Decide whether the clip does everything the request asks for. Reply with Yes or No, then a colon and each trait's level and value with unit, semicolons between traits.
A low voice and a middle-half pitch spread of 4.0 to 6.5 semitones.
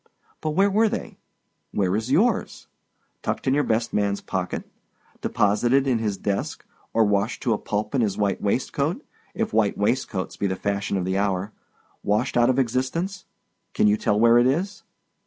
Yes: low, 110 Hz; average, 4.5 semitones